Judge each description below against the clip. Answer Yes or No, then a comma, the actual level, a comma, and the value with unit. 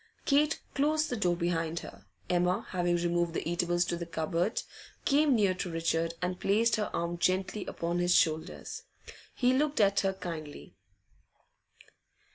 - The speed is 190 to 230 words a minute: No, average, 150 wpm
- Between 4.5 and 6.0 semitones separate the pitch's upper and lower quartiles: No, average, 3.8 semitones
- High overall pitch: No, medium, 175 Hz